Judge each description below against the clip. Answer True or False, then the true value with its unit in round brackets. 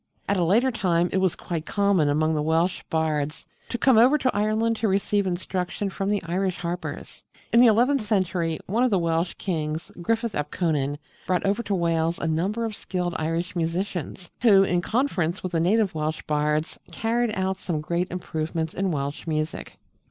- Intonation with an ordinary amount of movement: True (4.1 semitones)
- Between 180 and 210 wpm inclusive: True (185 wpm)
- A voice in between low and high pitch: True (180 Hz)